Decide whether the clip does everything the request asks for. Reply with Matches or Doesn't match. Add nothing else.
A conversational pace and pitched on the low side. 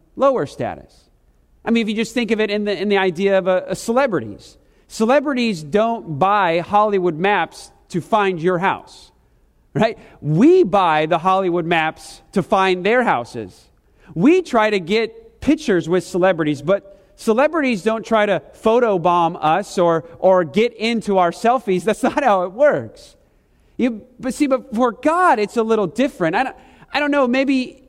Doesn't match